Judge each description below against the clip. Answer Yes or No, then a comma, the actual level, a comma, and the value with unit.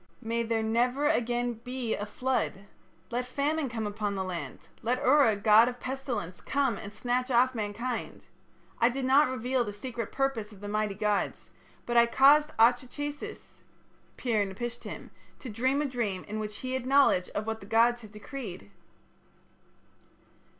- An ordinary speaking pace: Yes, average, 165 wpm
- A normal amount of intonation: Yes, average, 3.5 semitones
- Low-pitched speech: No, high, 235 Hz